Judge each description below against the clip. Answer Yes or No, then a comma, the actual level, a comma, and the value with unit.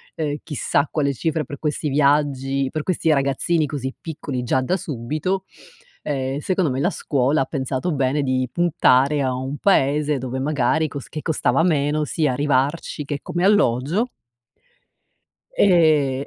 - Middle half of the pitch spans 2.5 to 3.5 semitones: Yes, average, 2.9 semitones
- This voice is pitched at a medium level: Yes, medium, 145 Hz